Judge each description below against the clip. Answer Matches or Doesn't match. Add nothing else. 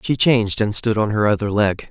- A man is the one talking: Matches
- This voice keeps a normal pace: Doesn't match